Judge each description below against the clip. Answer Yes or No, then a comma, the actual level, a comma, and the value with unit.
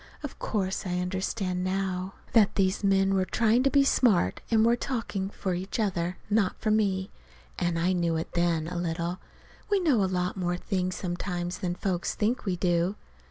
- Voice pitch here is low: No, medium, 185 Hz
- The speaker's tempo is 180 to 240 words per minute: Yes, average, 185 wpm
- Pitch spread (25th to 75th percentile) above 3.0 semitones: No, average, 2.7 semitones